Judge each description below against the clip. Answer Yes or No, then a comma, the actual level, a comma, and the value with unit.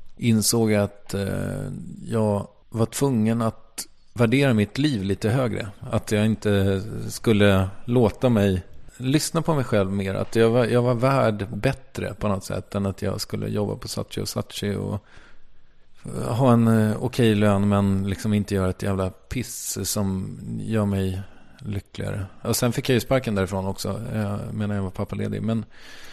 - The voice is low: Yes, low, 105 Hz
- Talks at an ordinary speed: Yes, average, 165 wpm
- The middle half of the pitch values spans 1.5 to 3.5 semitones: Yes, average, 2.9 semitones